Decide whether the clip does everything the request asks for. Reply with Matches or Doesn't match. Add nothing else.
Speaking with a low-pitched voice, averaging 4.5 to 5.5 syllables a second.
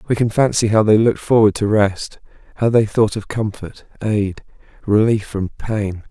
Matches